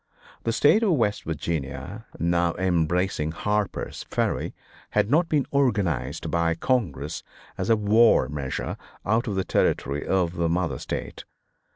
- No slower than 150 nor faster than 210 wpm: No, average, 140 wpm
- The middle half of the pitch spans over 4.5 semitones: Yes, wide, 5.4 semitones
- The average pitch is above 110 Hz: No, very low, 90 Hz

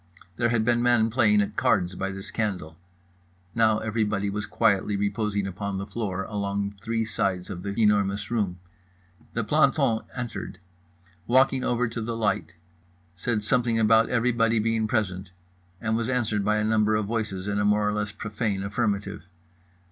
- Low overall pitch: Yes, low, 105 Hz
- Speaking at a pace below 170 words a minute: Yes, average, 160 wpm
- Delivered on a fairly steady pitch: Yes, narrow, 2.3 semitones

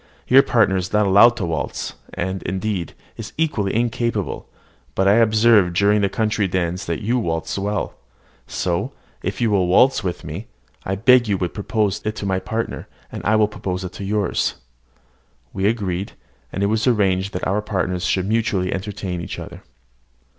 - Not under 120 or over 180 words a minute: Yes, average, 175 wpm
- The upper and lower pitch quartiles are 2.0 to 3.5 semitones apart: Yes, average, 2.8 semitones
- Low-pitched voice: Yes, low, 100 Hz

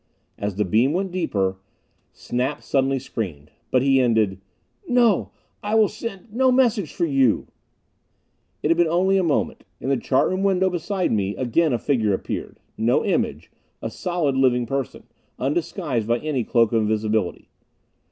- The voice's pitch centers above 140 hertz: No, low, 135 Hz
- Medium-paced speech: Yes, average, 160 wpm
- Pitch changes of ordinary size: No, wide, 8.0 semitones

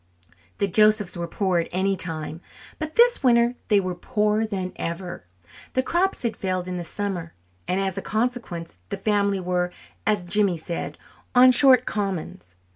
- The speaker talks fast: No, average, 165 wpm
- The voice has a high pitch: Yes, high, 195 Hz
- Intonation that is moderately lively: Yes, average, 3.8 semitones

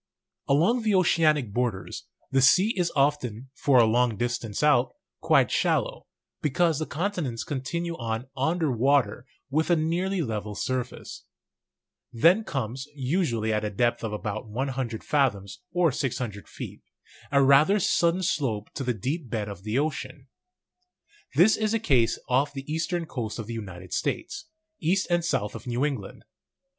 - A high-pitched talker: No, low, 135 Hz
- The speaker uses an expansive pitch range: Yes, wide, 6.3 semitones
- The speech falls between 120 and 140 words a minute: No, average, 155 wpm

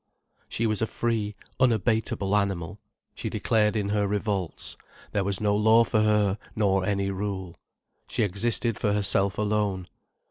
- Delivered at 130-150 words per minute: Yes, average, 145 wpm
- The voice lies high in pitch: No, low, 105 Hz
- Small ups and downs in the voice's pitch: Yes, narrow, 1.6 semitones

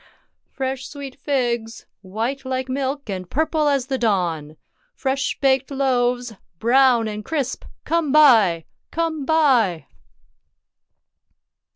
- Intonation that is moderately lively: Yes, average, 3.8 semitones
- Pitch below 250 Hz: No, very high, 260 Hz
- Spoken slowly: Yes, slow, 110 wpm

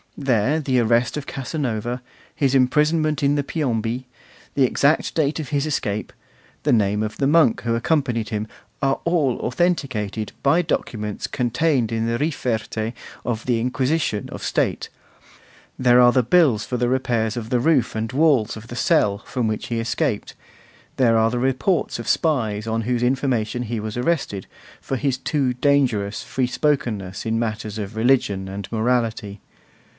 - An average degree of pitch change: Yes, average, 3.9 semitones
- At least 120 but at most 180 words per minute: Yes, average, 165 wpm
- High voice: No, low, 120 Hz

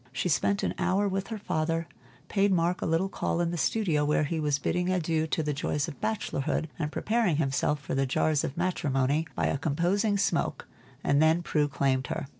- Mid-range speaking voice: Yes, medium, 160 Hz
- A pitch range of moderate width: Yes, average, 3.9 semitones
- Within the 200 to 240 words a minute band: Yes, fast, 205 wpm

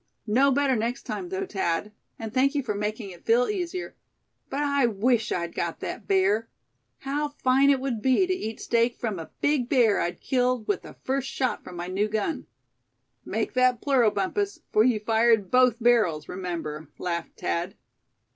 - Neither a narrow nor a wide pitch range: Yes, average, 4.8 semitones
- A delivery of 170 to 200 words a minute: Yes, average, 180 wpm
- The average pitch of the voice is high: Yes, high, 235 Hz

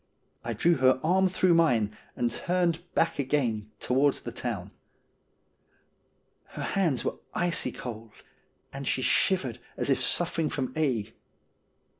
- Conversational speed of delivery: No, slow, 130 wpm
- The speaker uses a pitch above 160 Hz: No, medium, 140 Hz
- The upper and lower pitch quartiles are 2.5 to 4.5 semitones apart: No, wide, 5.6 semitones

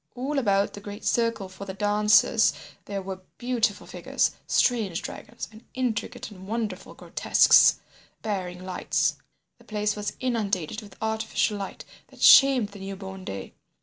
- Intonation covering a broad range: No, average, 2.7 semitones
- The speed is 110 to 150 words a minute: Yes, average, 145 wpm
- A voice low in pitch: No, high, 205 Hz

